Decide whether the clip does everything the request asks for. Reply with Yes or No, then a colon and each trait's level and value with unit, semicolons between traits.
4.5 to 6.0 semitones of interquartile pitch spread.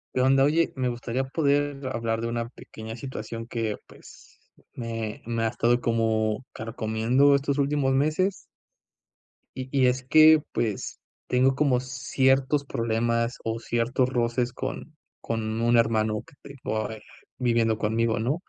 No: average, 2.9 semitones